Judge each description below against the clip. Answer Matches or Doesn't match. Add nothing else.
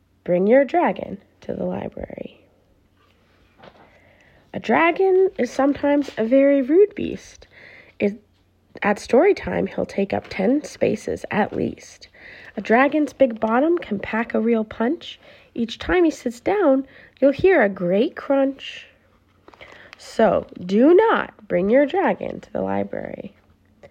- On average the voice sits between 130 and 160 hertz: Doesn't match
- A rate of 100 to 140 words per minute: Matches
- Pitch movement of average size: Doesn't match